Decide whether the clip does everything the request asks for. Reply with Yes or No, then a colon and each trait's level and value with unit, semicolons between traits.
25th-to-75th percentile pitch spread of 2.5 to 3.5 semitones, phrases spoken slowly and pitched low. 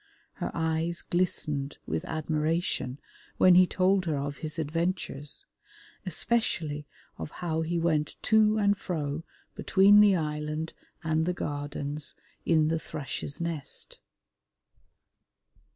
No: average, 3.0 semitones; slow, 115 wpm; medium, 160 Hz